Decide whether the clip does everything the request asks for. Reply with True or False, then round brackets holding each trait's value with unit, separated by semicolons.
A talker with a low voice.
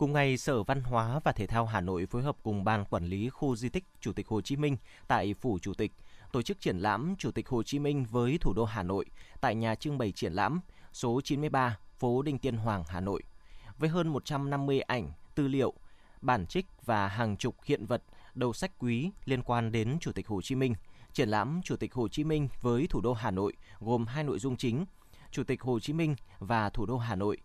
True (120 Hz)